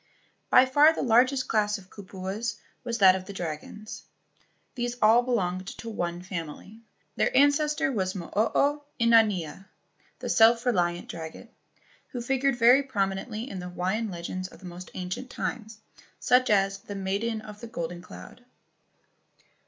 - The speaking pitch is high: Yes, high, 215 Hz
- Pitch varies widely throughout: No, average, 4.6 semitones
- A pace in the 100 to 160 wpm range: Yes, average, 150 wpm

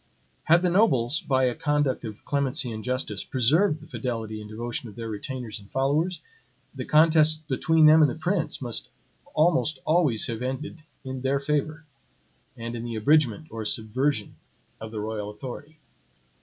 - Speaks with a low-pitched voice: Yes, low, 130 Hz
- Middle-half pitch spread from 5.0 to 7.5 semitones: Yes, average, 5.3 semitones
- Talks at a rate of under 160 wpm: No, average, 165 wpm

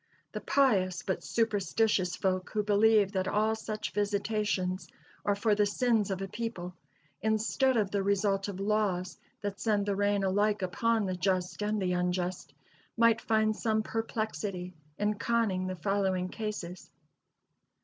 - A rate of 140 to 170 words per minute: Yes, average, 150 wpm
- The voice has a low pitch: No, high, 205 Hz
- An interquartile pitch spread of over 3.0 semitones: No, narrow, 2.5 semitones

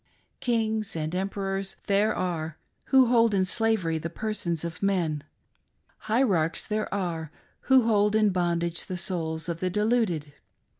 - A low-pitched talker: No, high, 190 Hz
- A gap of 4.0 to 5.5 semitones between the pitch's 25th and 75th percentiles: Yes, average, 4.4 semitones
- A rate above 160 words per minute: No, average, 140 wpm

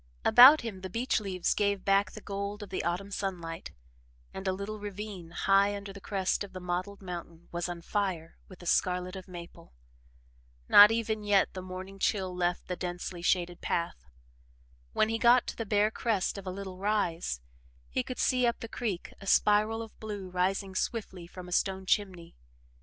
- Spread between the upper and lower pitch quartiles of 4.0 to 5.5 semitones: No, narrow, 2.4 semitones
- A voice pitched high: Yes, high, 195 Hz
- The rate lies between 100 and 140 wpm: No, average, 190 wpm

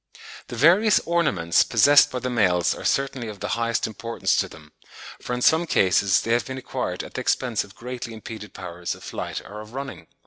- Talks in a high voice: No, low, 115 Hz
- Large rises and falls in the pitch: No, average, 4.5 semitones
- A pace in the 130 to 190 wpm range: No, fast, 205 wpm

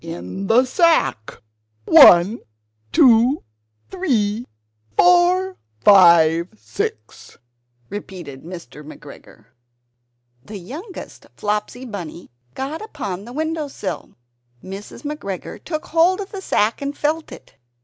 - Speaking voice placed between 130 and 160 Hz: No, high, 230 Hz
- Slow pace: Yes, slow, 100 wpm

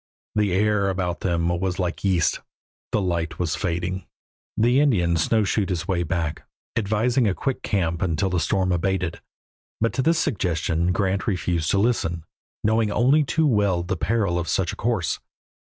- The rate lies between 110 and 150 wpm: No, average, 165 wpm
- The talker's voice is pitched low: Yes, very low, 95 Hz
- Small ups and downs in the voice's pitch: No, average, 3.7 semitones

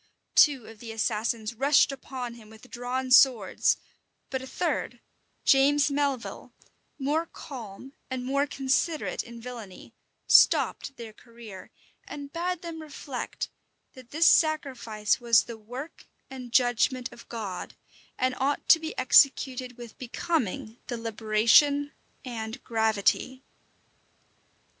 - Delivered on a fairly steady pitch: No, average, 3.5 semitones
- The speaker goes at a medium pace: No, slow, 120 wpm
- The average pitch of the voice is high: Yes, very high, 255 Hz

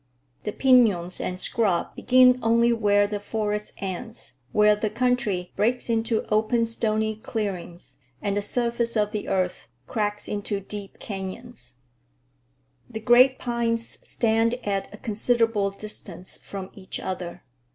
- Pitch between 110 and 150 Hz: No, high, 215 Hz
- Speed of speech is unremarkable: No, slow, 130 wpm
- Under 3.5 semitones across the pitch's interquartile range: Yes, average, 2.7 semitones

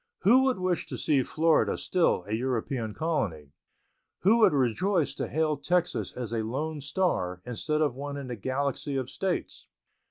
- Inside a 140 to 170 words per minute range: Yes, average, 165 wpm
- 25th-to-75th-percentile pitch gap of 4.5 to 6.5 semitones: Yes, wide, 5.6 semitones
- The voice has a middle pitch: Yes, medium, 145 Hz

